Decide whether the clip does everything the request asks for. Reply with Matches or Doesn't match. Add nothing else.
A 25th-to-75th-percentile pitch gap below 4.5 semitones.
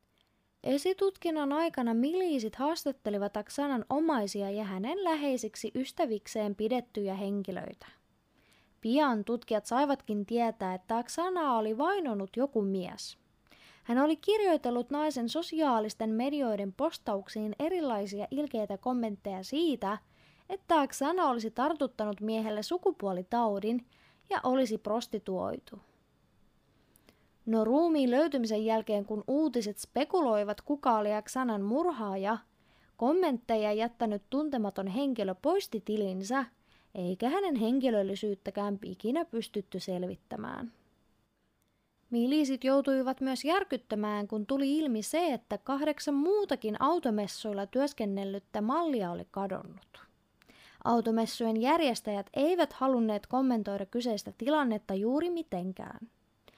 Doesn't match